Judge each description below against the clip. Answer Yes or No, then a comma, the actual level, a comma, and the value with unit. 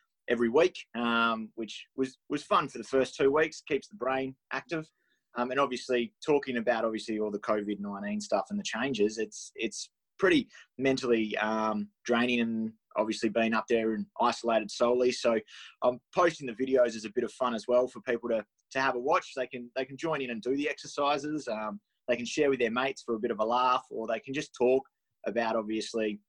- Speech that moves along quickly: Yes, fast, 215 wpm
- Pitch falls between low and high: No, low, 120 Hz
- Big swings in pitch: No, average, 3.0 semitones